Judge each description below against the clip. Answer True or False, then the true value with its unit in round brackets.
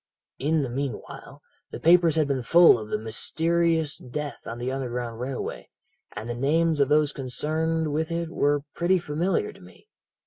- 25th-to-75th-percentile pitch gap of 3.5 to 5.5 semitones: True (4.3 semitones)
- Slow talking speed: False (170 wpm)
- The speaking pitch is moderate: True (150 Hz)